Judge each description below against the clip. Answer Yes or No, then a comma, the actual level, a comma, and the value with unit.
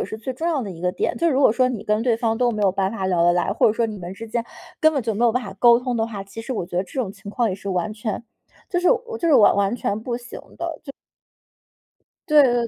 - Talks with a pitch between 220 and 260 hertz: Yes, high, 225 Hz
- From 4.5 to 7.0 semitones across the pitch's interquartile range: No, average, 4.1 semitones